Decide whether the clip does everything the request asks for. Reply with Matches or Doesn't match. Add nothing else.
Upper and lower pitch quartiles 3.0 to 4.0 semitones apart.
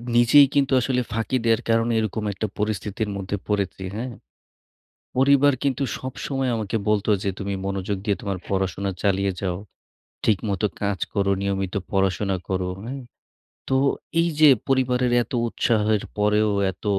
Matches